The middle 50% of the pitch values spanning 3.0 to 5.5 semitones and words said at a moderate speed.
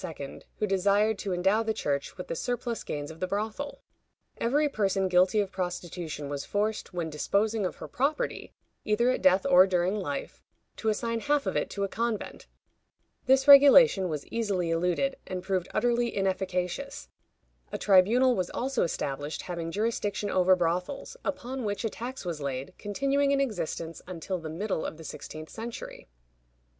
Yes: average, 4.7 semitones; average, 165 wpm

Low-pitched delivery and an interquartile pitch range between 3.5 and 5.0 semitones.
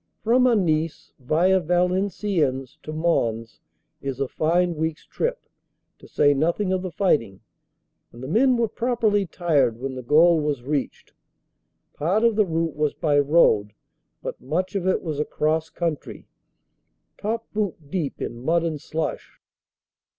No: medium, 160 Hz; average, 4.6 semitones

